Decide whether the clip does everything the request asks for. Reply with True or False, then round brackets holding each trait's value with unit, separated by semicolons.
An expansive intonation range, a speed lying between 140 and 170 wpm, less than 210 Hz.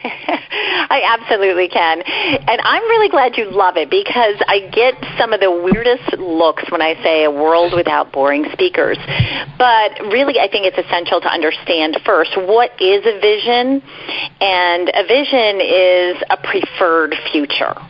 True (8.5 semitones; 155 wpm; 190 Hz)